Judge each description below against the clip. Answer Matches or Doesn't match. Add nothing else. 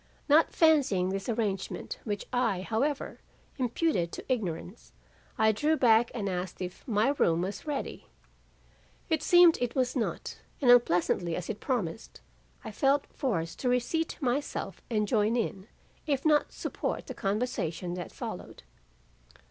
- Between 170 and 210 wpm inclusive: Doesn't match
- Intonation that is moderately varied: Doesn't match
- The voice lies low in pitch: Doesn't match